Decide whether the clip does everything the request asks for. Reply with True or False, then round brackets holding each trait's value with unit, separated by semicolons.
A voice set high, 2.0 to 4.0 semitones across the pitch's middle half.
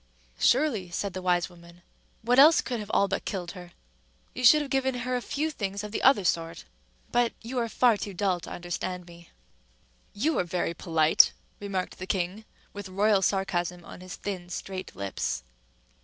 False (195 Hz; 4.7 semitones)